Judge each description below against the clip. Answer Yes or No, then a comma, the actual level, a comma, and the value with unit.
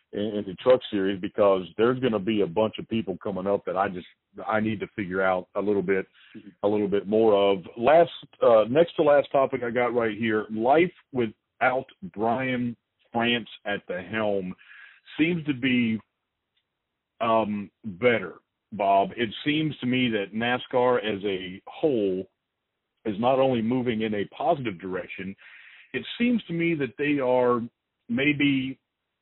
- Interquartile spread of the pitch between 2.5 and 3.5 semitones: No, average, 4.2 semitones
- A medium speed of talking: Yes, average, 160 wpm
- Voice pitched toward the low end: Yes, low, 115 Hz